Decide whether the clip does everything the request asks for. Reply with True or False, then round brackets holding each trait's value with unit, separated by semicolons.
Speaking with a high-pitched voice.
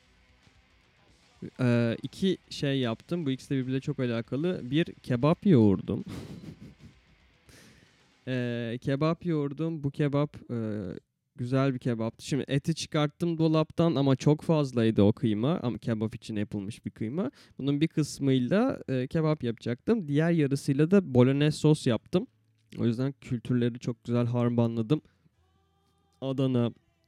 False (130 Hz)